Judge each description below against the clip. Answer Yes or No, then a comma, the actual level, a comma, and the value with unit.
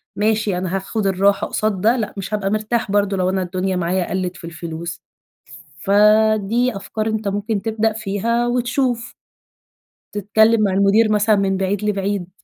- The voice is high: Yes, high, 205 Hz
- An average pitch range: No, narrow, 2.2 semitones